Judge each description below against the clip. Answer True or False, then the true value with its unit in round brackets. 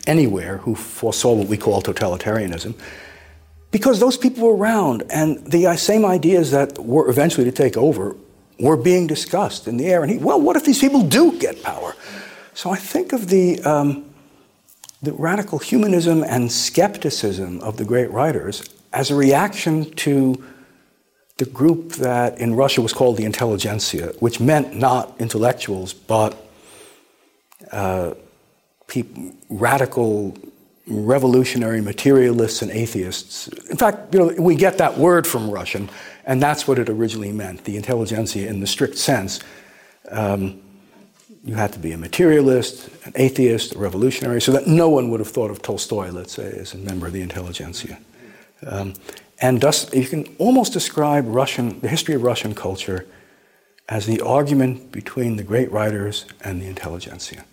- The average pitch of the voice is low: True (125 Hz)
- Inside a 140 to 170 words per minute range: True (155 wpm)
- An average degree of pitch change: False (6.8 semitones)